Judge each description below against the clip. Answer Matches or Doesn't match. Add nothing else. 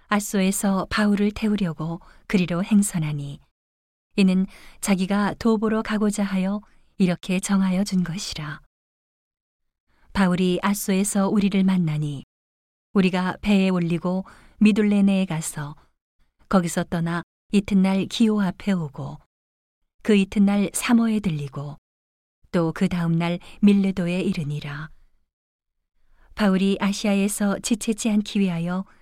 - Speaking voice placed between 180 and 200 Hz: Matches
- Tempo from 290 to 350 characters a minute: Doesn't match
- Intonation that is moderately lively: Matches